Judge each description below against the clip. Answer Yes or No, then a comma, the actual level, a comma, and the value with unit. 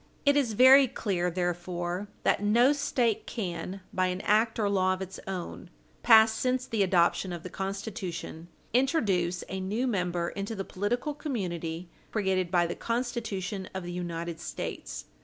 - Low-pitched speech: No, high, 195 Hz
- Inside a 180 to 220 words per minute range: No, average, 160 wpm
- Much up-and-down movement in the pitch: No, average, 4.4 semitones